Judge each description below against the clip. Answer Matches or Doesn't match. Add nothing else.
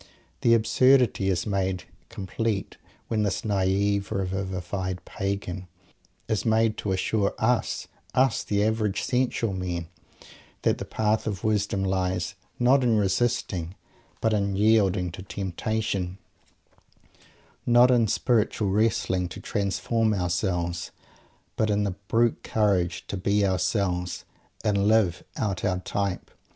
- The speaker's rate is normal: Doesn't match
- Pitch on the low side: Matches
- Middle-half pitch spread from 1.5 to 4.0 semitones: Matches